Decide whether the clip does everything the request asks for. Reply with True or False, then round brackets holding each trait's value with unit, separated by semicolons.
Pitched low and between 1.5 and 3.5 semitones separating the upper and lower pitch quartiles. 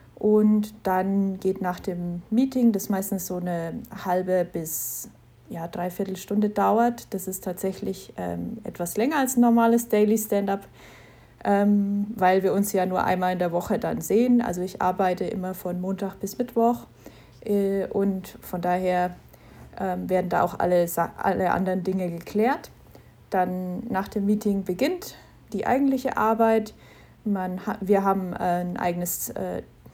False (195 Hz; 2.6 semitones)